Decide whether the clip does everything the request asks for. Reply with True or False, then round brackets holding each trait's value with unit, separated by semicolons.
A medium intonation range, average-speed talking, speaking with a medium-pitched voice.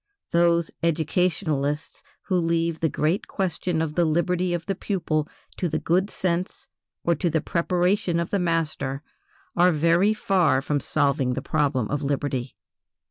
True (3.0 semitones; 150 wpm; 165 Hz)